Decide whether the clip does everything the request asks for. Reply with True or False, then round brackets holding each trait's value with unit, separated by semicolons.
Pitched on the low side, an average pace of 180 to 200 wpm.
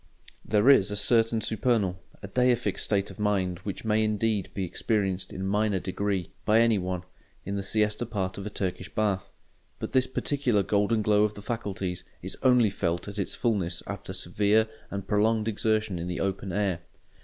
True (105 Hz; 185 wpm)